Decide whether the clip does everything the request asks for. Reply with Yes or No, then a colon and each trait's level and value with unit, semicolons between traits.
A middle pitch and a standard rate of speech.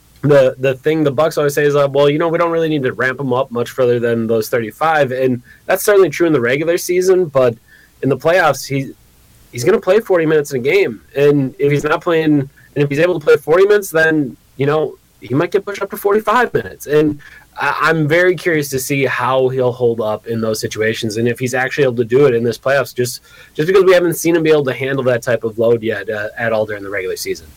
No: medium, 145 Hz; fast, 260 wpm